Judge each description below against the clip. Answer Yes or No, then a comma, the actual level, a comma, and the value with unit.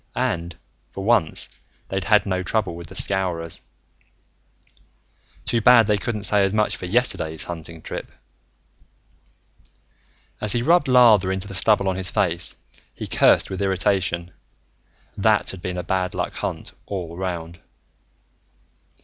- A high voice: No, very low, 95 Hz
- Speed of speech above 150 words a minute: No, average, 140 wpm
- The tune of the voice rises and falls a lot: No, average, 3.3 semitones